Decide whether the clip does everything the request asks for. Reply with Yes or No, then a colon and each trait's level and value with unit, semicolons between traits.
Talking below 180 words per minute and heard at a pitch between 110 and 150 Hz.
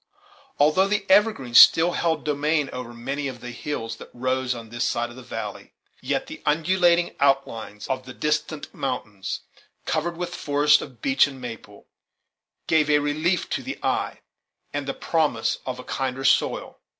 Yes: average, 165 wpm; medium, 140 Hz